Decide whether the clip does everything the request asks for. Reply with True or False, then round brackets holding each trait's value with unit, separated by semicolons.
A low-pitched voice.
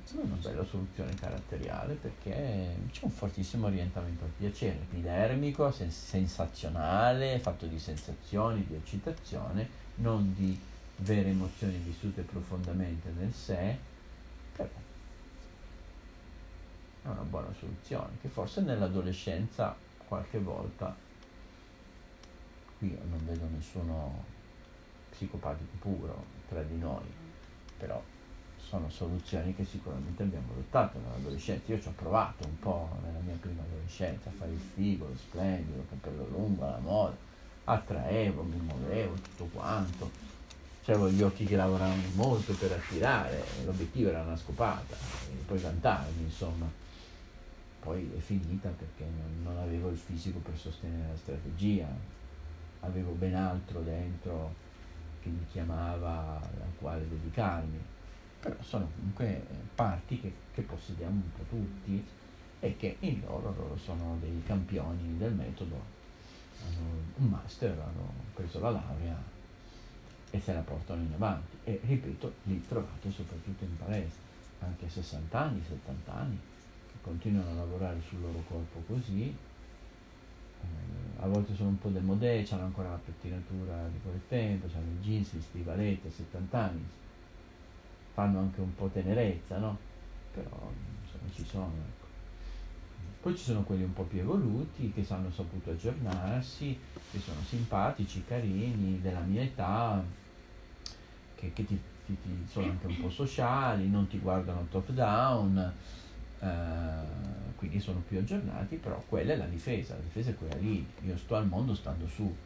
True (90 Hz)